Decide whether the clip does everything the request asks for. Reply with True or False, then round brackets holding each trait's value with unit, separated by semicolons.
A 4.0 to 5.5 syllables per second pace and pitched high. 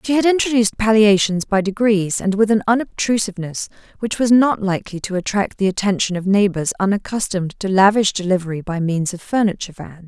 False (6.0 syllables/s; 200 Hz)